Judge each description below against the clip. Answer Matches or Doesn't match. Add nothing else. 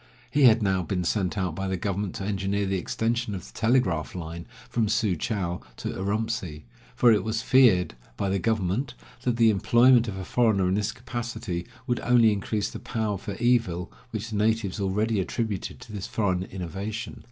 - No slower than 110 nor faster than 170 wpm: Doesn't match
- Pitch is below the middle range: Matches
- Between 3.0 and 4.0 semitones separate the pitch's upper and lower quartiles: Matches